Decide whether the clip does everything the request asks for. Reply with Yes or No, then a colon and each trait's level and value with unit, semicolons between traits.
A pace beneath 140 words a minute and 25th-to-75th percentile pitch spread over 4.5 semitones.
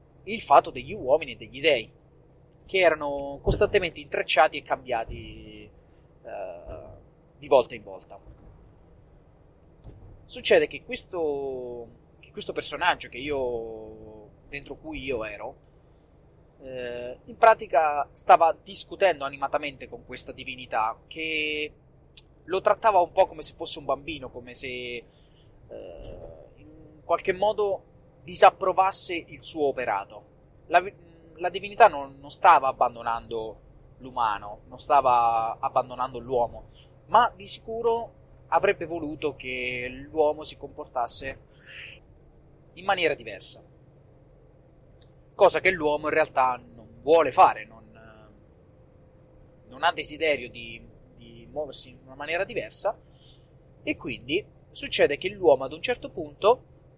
Yes: slow, 115 wpm; wide, 5.4 semitones